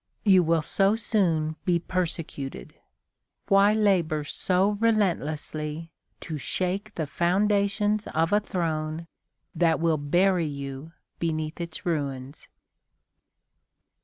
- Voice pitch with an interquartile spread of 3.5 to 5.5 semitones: Yes, average, 4.2 semitones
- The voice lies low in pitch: No, medium, 170 Hz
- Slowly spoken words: Yes, slow, 105 wpm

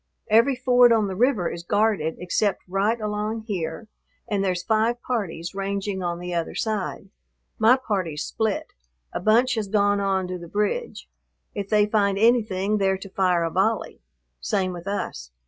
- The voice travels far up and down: No, average, 3.0 semitones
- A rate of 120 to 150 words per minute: No, average, 165 wpm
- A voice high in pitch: Yes, high, 200 Hz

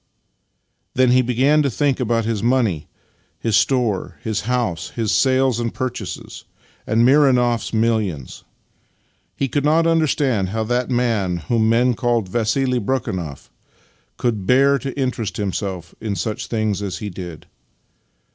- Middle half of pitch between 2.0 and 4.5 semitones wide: Yes, average, 3.7 semitones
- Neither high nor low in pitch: No, low, 115 Hz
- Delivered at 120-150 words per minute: Yes, average, 140 wpm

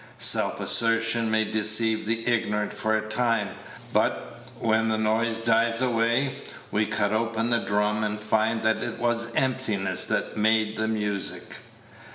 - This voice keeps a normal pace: Yes, average, 150 wpm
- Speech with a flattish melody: Yes, narrow, 1.2 semitones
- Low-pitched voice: Yes, low, 110 Hz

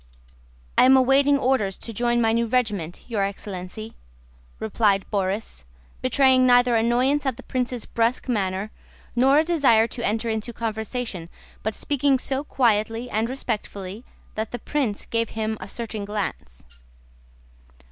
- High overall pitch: Yes, high, 230 Hz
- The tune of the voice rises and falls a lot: No, average, 3.3 semitones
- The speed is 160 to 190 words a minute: No, average, 140 wpm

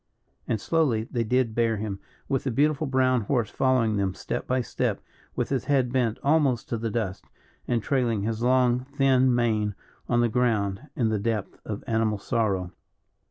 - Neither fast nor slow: Yes, average, 175 wpm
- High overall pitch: No, low, 120 Hz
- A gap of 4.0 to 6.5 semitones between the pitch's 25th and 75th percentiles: No, average, 3.0 semitones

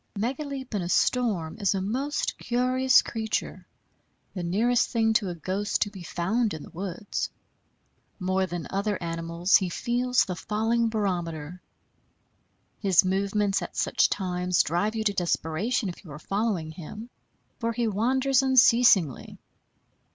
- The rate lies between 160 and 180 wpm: No, average, 145 wpm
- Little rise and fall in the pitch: No, average, 4.6 semitones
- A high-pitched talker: Yes, high, 205 Hz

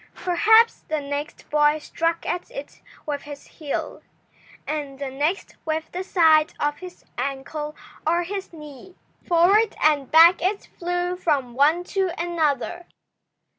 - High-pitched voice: Yes, very high, 320 Hz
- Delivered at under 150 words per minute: Yes, slow, 135 wpm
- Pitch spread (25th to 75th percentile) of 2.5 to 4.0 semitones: Yes, average, 3.3 semitones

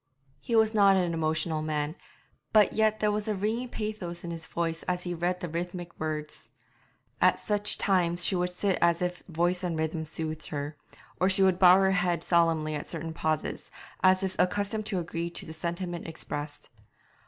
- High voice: No, medium, 175 Hz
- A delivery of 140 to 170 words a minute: No, average, 190 wpm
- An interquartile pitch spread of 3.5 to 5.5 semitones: No, average, 2.9 semitones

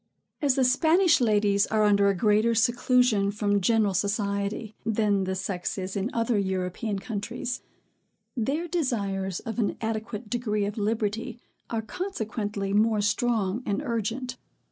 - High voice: Yes, high, 215 Hz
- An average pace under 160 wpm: Yes, average, 140 wpm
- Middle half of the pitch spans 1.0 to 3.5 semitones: Yes, average, 2.8 semitones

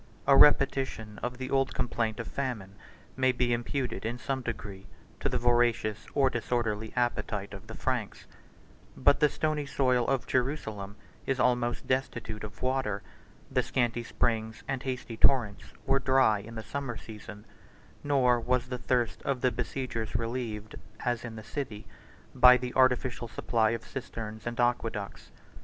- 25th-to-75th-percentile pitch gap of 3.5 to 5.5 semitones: No, average, 2.8 semitones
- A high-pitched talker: No, low, 120 Hz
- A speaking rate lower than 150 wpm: No, average, 155 wpm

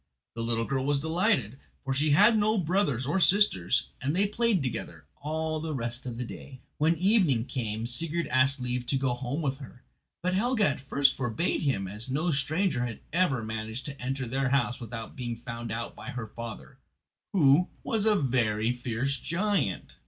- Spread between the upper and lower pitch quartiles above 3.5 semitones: Yes, wide, 5.5 semitones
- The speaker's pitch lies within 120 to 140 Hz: Yes, low, 135 Hz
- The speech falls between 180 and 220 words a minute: Yes, average, 185 wpm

